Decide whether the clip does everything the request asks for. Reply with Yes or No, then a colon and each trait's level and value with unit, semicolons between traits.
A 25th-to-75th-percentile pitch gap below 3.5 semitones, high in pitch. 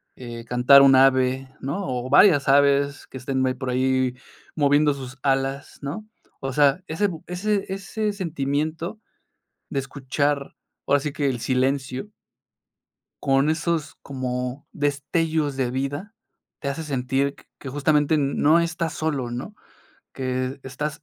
No: average, 2.7 semitones; medium, 140 Hz